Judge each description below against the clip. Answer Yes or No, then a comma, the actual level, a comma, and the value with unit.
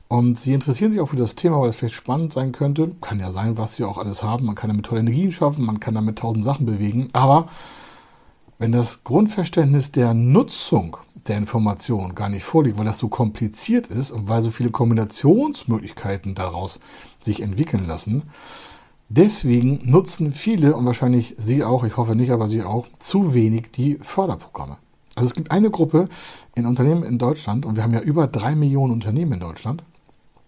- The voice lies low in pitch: Yes, low, 120 Hz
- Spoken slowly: No, average, 185 wpm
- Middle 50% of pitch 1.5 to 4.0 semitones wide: No, average, 4.9 semitones